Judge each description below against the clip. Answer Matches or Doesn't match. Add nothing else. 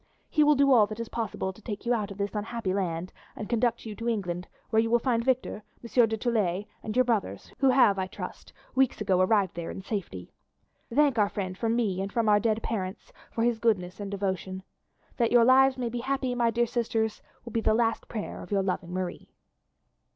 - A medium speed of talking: Doesn't match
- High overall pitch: Matches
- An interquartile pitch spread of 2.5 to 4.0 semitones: Matches